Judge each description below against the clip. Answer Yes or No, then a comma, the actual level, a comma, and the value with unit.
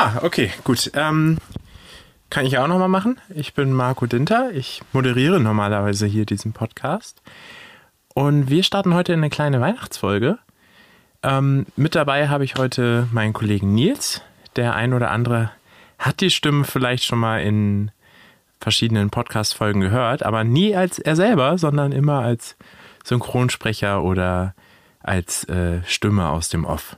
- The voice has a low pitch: Yes, low, 125 Hz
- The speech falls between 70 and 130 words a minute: No, average, 145 wpm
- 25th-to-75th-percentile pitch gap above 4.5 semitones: Yes, average, 5.3 semitones